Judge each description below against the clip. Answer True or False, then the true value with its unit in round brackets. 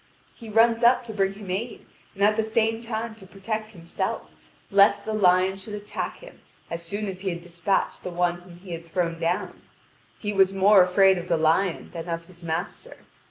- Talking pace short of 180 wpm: False (205 wpm)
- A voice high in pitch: True (195 Hz)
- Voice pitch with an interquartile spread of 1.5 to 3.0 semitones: False (3.5 semitones)